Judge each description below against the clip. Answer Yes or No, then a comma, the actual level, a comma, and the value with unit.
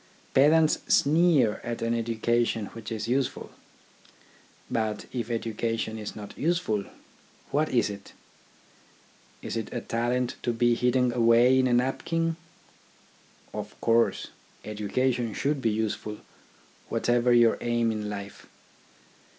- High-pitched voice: No, low, 120 Hz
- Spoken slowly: Yes, slow, 120 wpm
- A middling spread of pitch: No, narrow, 2.3 semitones